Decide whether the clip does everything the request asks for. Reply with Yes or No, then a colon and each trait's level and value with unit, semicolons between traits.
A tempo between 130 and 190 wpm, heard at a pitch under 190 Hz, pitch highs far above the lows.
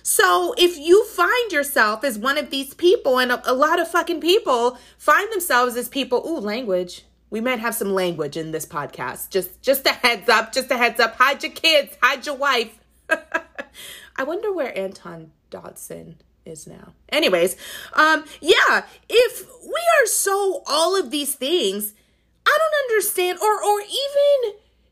No: average, 165 wpm; very high, 280 Hz; wide, 7.4 semitones